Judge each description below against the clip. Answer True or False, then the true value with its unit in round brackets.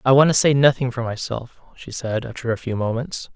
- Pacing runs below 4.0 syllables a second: False (5.5 syllables/s)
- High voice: False (125 Hz)